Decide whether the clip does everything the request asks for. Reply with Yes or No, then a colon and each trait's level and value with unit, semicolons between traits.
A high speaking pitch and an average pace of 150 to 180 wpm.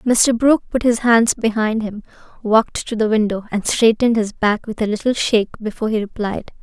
No: high, 220 Hz; average, 200 wpm